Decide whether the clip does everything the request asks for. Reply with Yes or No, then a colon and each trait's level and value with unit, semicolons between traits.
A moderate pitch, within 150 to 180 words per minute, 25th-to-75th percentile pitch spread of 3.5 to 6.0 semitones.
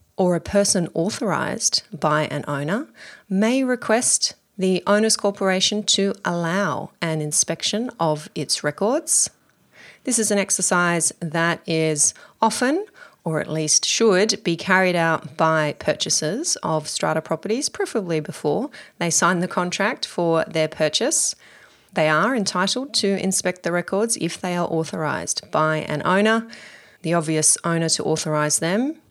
No: medium, 180 Hz; average, 140 wpm; average, 4.8 semitones